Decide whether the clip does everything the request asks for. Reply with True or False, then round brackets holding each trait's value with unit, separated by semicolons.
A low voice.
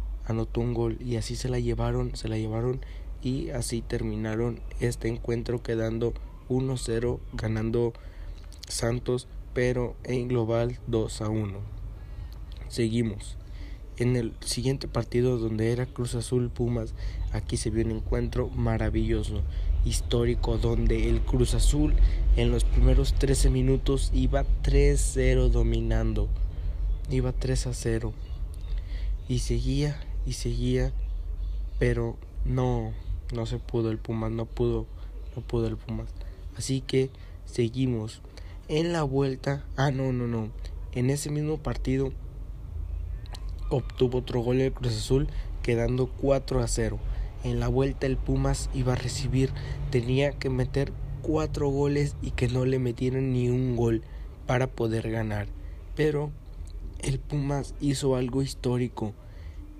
True (120 Hz)